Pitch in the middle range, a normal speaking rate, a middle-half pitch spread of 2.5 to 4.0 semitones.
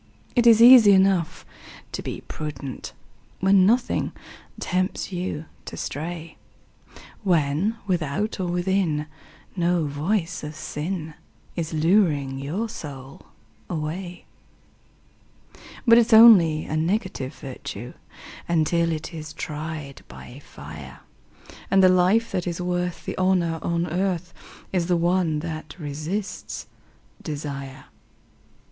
No: medium, 170 Hz; slow, 115 wpm; average, 3.7 semitones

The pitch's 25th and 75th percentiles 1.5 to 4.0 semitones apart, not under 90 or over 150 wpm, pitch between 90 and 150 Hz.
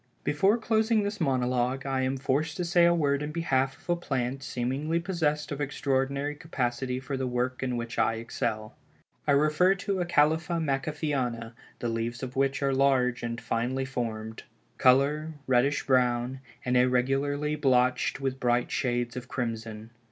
No: average, 3.3 semitones; average, 160 wpm; low, 135 Hz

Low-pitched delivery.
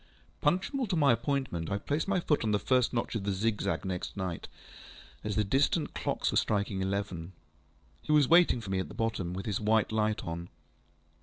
Yes: low, 105 Hz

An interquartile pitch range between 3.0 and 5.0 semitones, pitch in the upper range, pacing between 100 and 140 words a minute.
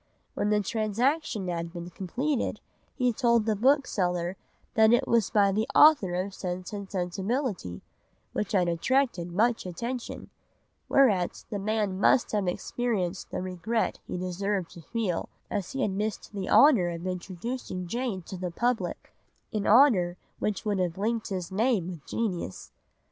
No: average, 4.5 semitones; high, 200 Hz; average, 155 wpm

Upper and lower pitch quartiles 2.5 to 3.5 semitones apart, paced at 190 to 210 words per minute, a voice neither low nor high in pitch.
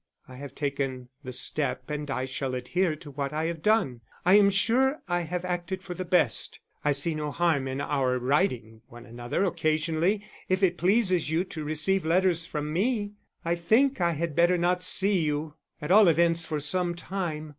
No: average, 4.2 semitones; average, 195 wpm; medium, 165 Hz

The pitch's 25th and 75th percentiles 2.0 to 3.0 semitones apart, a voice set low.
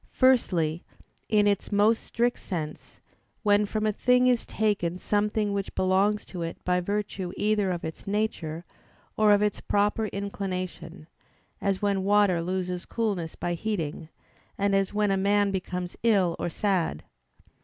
No: narrow, 2.6 semitones; high, 200 Hz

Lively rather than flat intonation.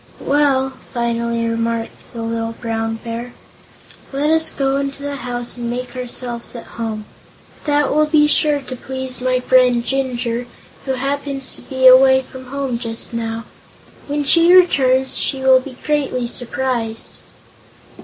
No: average, 2.8 semitones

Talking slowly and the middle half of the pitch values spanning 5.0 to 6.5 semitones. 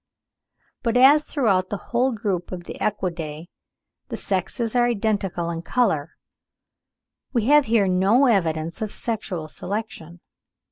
Yes: slow, 130 wpm; wide, 5.4 semitones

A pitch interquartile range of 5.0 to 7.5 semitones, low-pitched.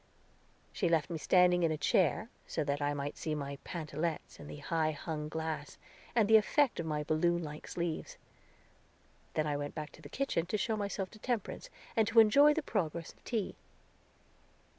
No: wide, 5.5 semitones; medium, 165 Hz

